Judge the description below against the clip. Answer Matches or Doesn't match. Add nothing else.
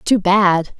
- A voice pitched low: Doesn't match